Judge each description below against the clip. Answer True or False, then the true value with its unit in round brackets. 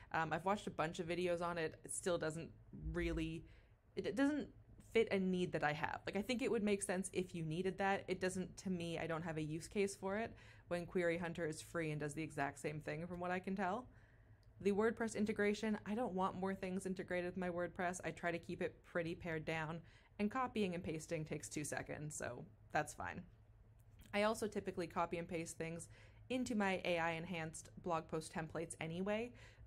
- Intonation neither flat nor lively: True (3.3 semitones)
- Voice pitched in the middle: True (170 Hz)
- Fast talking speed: True (215 wpm)